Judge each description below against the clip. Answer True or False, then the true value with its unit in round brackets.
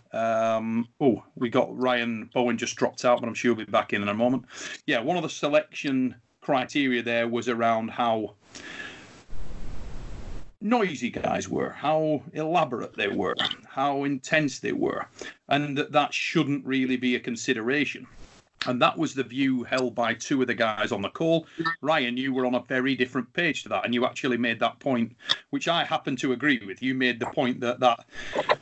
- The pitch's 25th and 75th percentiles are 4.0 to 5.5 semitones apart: False (2.8 semitones)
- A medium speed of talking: True (190 wpm)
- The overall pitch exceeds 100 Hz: True (125 Hz)